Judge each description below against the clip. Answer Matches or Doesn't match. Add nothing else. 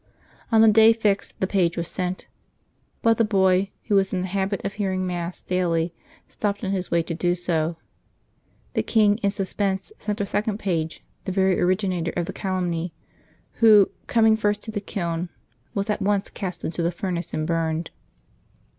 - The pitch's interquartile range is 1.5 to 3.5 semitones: Matches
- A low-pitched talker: Doesn't match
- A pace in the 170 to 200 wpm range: Matches